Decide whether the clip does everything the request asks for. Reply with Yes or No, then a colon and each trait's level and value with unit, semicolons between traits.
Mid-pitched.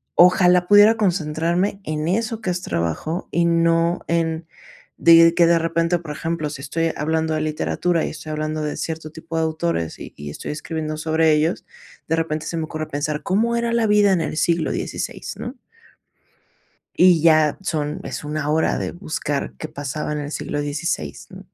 Yes: medium, 160 Hz